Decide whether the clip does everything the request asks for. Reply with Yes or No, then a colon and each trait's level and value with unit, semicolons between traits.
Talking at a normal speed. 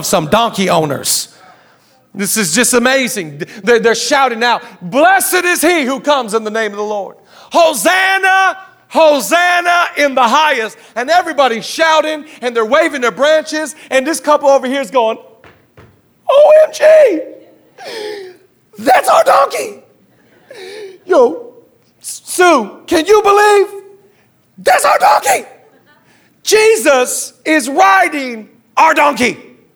No: slow, 120 wpm